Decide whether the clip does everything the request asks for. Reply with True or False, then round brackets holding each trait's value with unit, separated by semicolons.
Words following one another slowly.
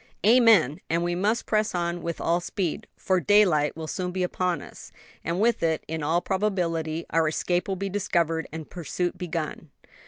False (180 wpm)